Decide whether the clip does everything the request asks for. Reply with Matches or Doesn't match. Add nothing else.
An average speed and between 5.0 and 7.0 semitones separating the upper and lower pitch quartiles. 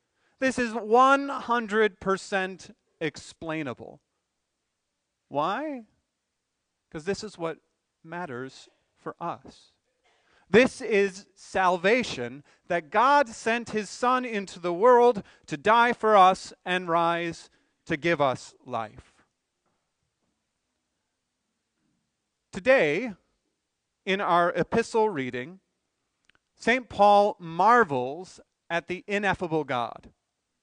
Doesn't match